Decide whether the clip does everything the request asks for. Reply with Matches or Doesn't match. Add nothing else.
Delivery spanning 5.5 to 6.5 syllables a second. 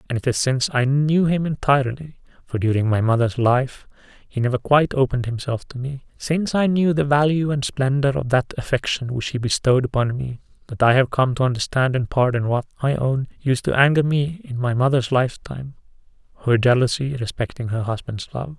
Matches